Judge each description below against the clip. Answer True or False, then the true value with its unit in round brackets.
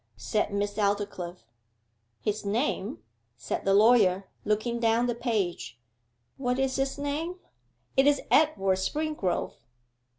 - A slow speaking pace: True (125 wpm)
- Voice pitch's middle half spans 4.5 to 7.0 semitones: True (5.6 semitones)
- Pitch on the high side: True (215 Hz)